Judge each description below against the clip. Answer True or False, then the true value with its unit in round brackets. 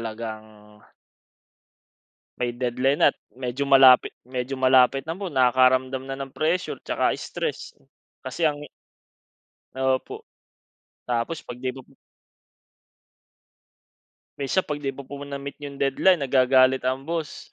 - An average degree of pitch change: False (1.9 semitones)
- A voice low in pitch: True (130 Hz)